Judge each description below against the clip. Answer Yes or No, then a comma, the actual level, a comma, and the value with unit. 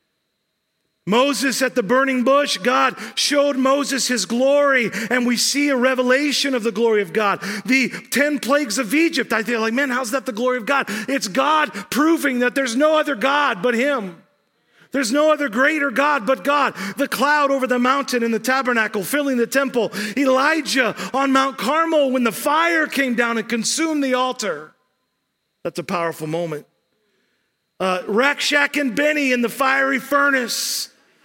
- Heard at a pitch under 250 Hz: No, very high, 265 Hz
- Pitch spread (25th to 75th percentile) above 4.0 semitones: No, average, 3.3 semitones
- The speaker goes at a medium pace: Yes, average, 170 wpm